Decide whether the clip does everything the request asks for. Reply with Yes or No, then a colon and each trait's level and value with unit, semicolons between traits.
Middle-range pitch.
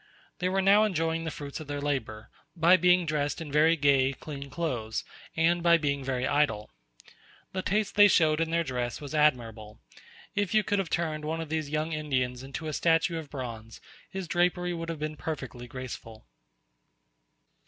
Yes: medium, 155 Hz